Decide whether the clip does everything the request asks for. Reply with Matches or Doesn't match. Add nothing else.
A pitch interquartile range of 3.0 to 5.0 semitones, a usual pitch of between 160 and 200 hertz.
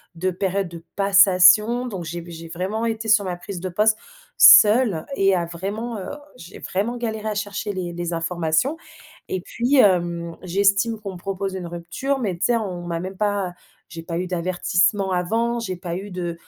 Matches